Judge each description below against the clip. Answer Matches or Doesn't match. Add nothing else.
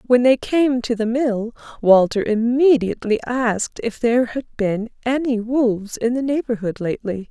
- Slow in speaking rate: Doesn't match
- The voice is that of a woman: Matches